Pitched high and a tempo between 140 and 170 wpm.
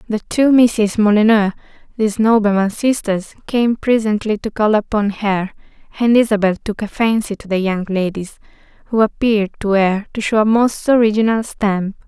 Yes: high, 215 Hz; average, 160 wpm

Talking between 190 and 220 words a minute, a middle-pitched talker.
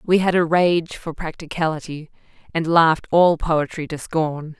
No: average, 155 wpm; medium, 160 Hz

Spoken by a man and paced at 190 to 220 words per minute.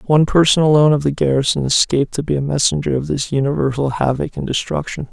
Yes: male; average, 200 wpm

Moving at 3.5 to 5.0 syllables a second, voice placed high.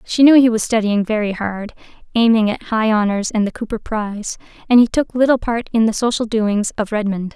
No: 5.4 syllables/s; high, 220 Hz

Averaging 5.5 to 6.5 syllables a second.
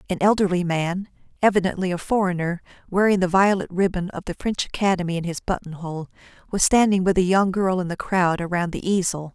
Yes: 5.9 syllables/s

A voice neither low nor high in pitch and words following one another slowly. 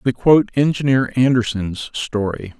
No: low, 120 Hz; slow, 115 wpm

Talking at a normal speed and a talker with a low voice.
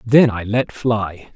Yes: average, 175 wpm; low, 110 Hz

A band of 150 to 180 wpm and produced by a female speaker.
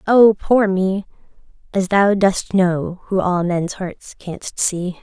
Yes: average, 155 wpm; female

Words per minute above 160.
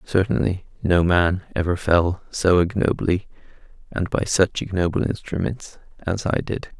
No: slow, 135 wpm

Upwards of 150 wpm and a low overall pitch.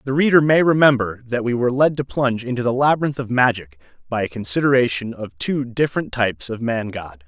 Yes: fast, 205 wpm; low, 125 Hz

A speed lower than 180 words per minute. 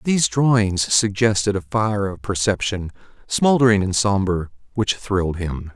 Yes: slow, 135 wpm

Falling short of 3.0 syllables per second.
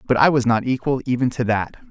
No: 6.1 syllables/s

